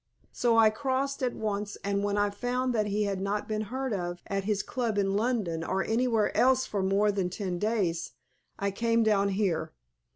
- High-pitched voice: Yes, high, 205 Hz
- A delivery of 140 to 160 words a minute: No, average, 195 wpm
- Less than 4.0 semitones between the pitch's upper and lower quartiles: Yes, average, 2.8 semitones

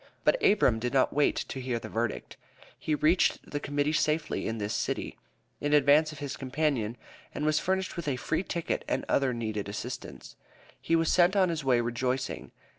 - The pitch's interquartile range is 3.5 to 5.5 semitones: Yes, average, 4.2 semitones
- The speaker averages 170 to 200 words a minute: Yes, average, 190 wpm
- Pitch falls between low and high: Yes, medium, 145 Hz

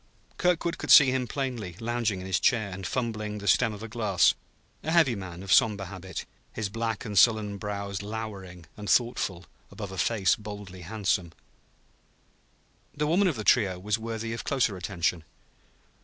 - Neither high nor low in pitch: No, low, 105 Hz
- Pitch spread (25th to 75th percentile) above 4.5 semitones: No, average, 3.4 semitones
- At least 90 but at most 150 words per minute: No, average, 170 wpm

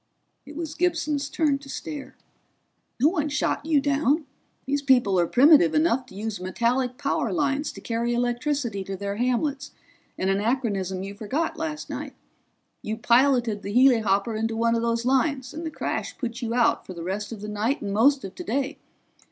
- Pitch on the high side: Yes, high, 245 Hz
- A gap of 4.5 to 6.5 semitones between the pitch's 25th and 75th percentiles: Yes, average, 4.9 semitones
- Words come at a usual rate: Yes, average, 180 wpm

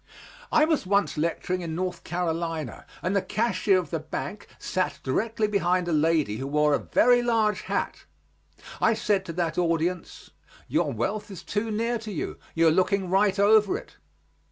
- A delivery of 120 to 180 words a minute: Yes, average, 175 wpm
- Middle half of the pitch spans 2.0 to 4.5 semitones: Yes, average, 4.2 semitones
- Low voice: No, medium, 185 Hz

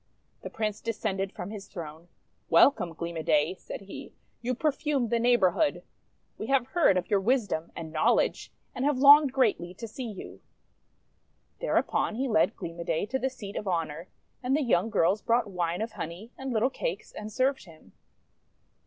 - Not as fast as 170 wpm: No, average, 185 wpm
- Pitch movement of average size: No, wide, 6.4 semitones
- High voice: Yes, high, 215 Hz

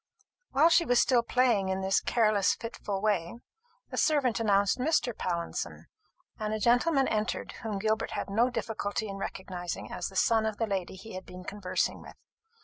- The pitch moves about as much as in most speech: Yes, average, 3.5 semitones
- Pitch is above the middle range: Yes, high, 215 Hz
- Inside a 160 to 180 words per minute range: Yes, average, 175 wpm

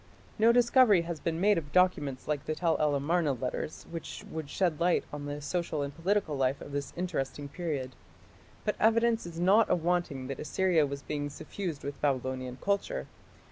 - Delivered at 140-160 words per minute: No, average, 180 wpm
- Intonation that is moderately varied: Yes, average, 4.3 semitones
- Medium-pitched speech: Yes, medium, 160 Hz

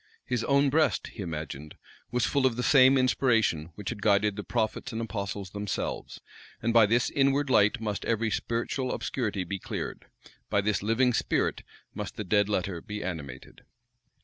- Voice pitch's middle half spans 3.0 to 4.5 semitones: Yes, average, 3.8 semitones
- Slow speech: No, average, 170 wpm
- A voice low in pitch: Yes, low, 110 Hz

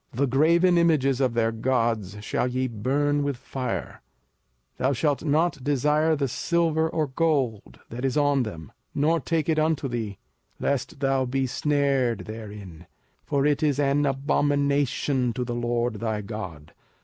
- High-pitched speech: No, low, 135 Hz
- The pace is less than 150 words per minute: No, average, 155 wpm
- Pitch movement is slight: No, average, 3.6 semitones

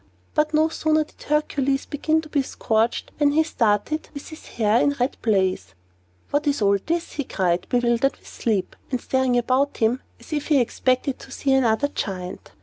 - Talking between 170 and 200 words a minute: Yes, average, 190 wpm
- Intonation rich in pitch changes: No, average, 4.9 semitones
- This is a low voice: No, very high, 265 Hz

